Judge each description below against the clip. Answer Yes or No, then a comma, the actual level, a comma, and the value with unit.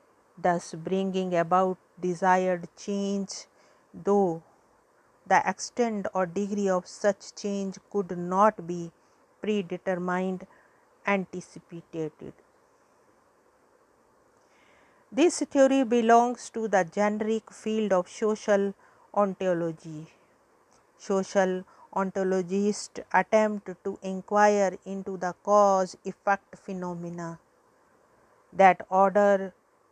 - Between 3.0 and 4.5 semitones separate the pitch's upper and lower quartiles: No, narrow, 2.6 semitones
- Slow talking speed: Yes, slow, 80 wpm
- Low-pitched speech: No, high, 195 Hz